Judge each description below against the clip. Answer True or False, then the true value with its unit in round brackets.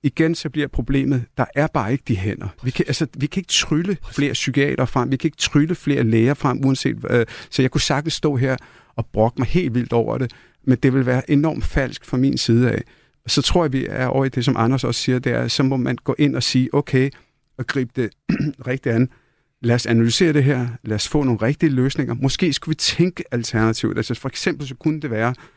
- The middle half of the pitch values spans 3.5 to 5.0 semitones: False (3.1 semitones)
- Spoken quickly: True (245 wpm)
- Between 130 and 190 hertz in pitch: True (135 Hz)